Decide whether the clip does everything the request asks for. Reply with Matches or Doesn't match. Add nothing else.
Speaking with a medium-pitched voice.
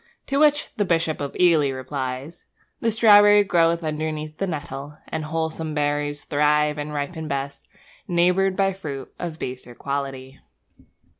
Matches